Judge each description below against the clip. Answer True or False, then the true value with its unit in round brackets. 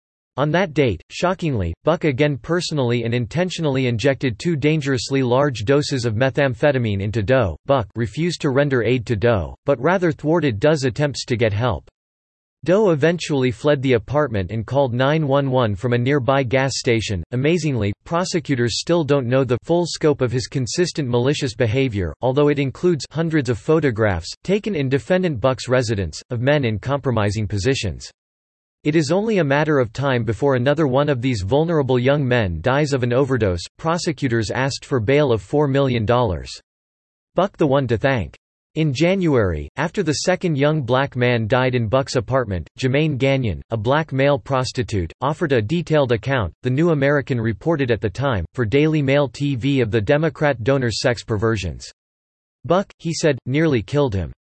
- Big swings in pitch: False (4.2 semitones)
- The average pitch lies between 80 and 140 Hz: True (135 Hz)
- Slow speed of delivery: False (165 wpm)